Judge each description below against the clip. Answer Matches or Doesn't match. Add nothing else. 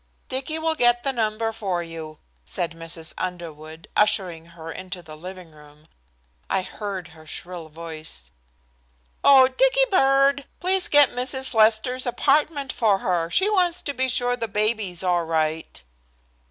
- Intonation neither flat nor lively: Doesn't match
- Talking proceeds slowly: Doesn't match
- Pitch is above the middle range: Matches